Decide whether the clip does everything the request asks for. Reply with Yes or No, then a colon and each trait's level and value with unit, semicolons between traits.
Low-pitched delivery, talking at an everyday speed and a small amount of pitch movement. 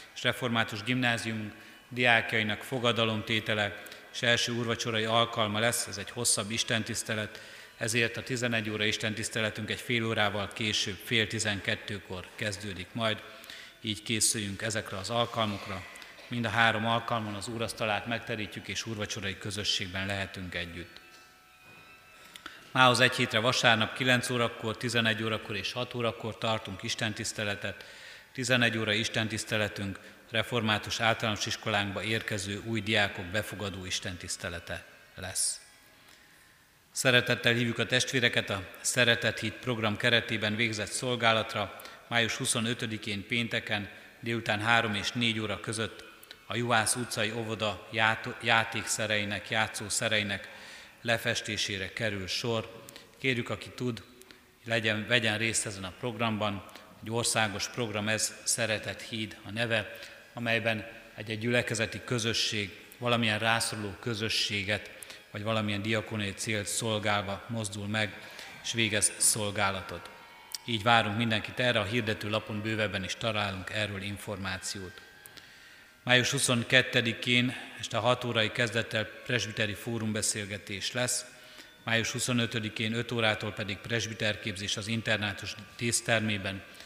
Yes: low, 110 Hz; average, 115 wpm; narrow, 2.0 semitones